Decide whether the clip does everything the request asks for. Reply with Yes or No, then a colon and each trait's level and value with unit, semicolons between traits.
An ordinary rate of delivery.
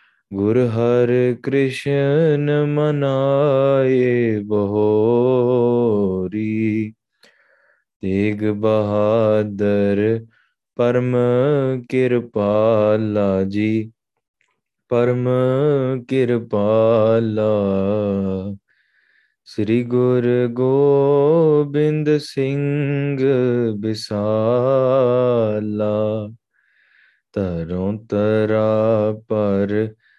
No: slow, 40 wpm